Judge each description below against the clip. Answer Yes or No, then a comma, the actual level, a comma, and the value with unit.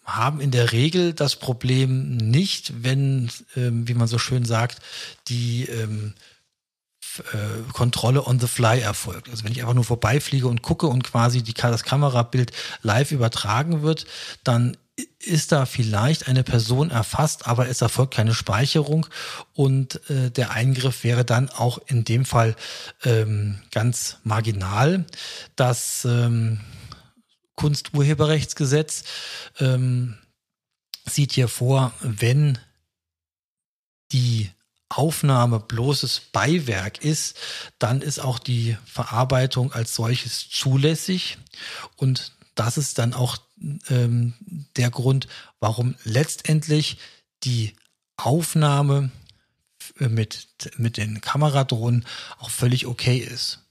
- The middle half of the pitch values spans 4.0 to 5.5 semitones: No, average, 3.2 semitones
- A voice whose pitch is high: No, low, 125 Hz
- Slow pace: Yes, slow, 120 wpm